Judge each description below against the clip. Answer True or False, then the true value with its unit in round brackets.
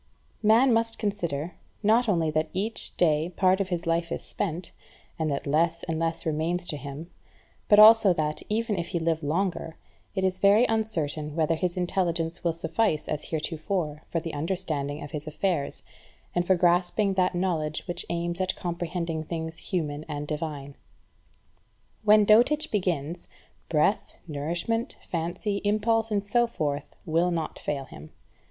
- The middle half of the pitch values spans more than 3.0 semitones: True (4.0 semitones)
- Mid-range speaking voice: True (170 Hz)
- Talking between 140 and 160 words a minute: True (155 wpm)